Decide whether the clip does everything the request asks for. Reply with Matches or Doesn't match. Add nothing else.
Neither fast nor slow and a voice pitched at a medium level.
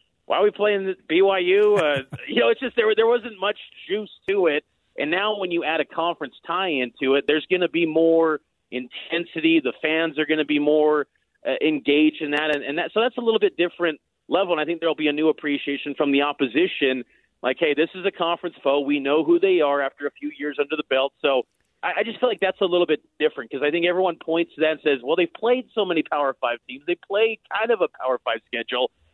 Doesn't match